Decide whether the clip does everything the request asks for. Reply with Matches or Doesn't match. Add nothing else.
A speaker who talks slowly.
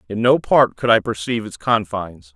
Doesn't match